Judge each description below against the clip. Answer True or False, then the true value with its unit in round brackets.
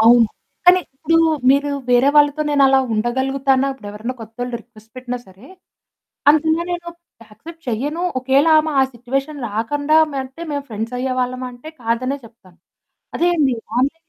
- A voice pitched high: True (260 Hz)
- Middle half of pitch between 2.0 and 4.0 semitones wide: True (3.6 semitones)